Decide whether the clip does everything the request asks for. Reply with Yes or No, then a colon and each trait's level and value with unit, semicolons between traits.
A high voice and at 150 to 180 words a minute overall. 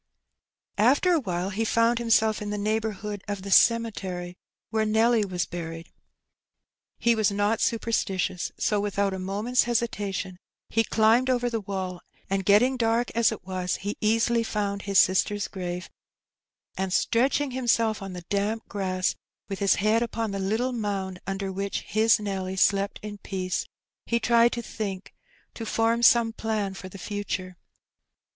Yes: high, 205 Hz; average, 160 wpm